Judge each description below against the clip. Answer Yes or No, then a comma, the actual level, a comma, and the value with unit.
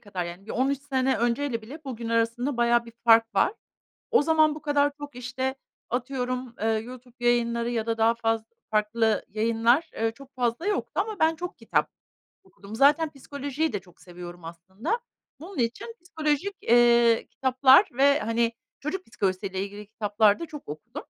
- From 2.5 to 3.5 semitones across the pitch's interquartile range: No, average, 4.1 semitones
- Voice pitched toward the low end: No, high, 240 Hz